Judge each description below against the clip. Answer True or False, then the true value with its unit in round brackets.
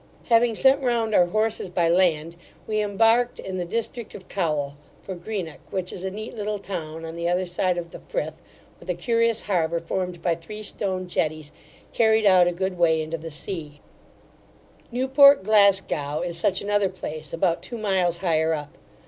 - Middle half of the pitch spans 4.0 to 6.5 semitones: True (4.3 semitones)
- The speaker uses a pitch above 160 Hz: True (185 Hz)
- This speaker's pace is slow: False (180 wpm)